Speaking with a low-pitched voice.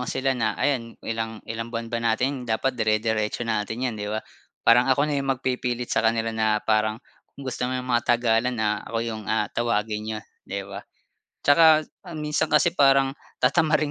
Yes: low, 115 Hz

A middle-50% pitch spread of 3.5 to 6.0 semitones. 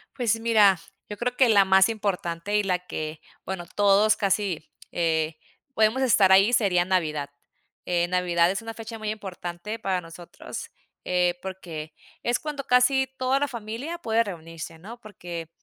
Yes: average, 4.5 semitones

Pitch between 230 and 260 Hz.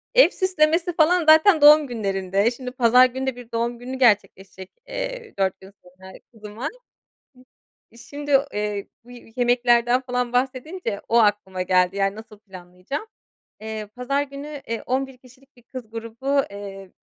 Yes: high, 245 Hz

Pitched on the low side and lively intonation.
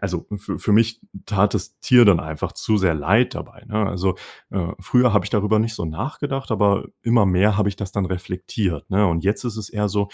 No: low, 100 Hz; average, 2.8 semitones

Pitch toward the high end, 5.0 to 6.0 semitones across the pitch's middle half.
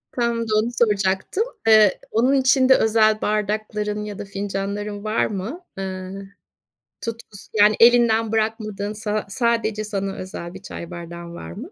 No: high, 215 Hz; narrow, 2.4 semitones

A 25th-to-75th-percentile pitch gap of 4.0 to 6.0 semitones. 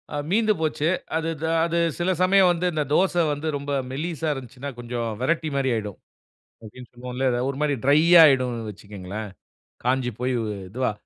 Yes: average, 4.9 semitones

